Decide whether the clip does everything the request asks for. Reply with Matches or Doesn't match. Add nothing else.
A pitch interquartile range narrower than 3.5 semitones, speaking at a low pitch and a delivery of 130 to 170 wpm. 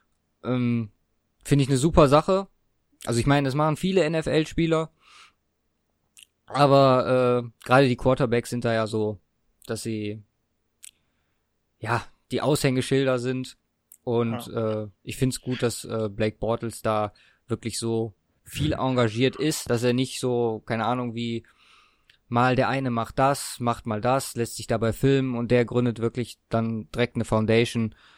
Matches